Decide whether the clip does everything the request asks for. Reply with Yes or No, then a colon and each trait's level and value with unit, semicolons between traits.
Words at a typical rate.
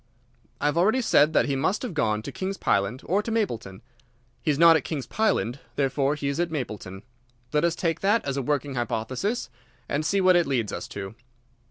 No: fast, 210 wpm